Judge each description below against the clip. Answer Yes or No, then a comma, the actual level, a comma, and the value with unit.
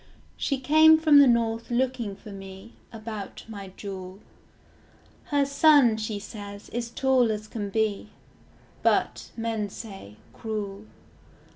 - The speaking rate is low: Yes, slow, 125 wpm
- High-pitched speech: Yes, high, 220 Hz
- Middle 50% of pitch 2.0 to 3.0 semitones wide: No, average, 3.6 semitones